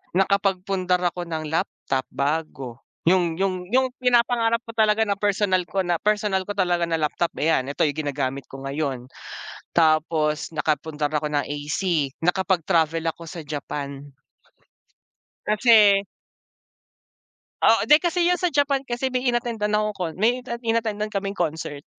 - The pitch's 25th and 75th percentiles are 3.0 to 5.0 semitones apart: No, wide, 5.5 semitones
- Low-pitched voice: No, medium, 180 Hz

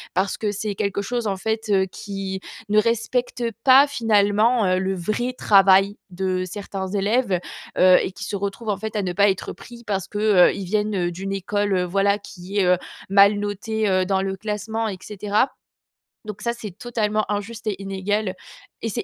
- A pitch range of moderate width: No, narrow, 2.1 semitones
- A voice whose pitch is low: No, high, 205 Hz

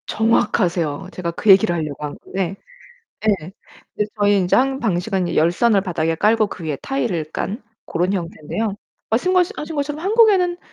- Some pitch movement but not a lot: No, wide, 6.1 semitones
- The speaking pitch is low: No, high, 195 Hz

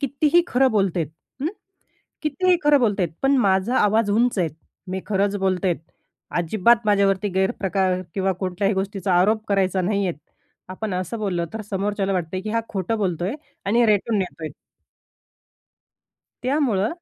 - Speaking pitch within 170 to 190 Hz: No, high, 200 Hz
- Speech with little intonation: No, average, 3.2 semitones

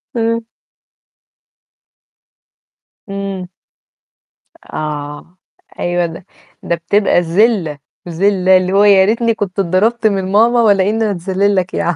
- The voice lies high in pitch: Yes, high, 195 Hz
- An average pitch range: Yes, average, 3.1 semitones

